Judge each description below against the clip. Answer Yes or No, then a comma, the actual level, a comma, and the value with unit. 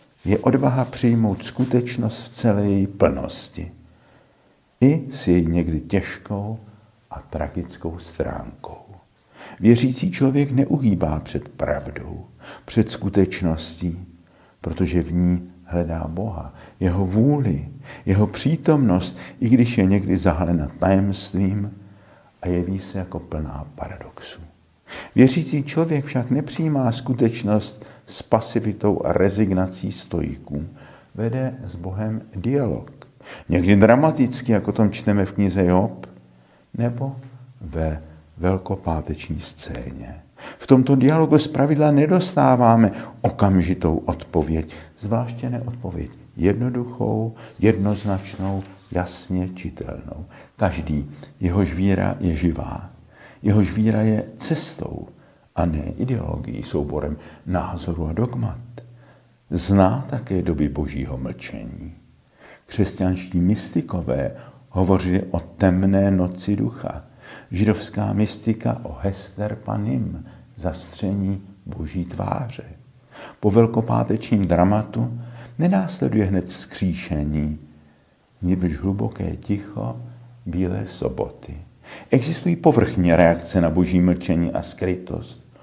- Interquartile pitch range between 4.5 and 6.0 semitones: Yes, average, 5.0 semitones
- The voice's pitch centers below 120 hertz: Yes, low, 100 Hz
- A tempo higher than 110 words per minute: No, slow, 95 wpm